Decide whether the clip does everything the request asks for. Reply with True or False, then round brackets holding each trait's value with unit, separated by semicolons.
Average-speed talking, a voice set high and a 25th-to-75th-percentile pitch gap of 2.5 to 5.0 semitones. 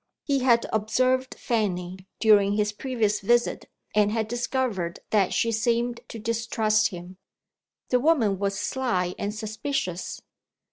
False (130 wpm; 220 Hz; 3.0 semitones)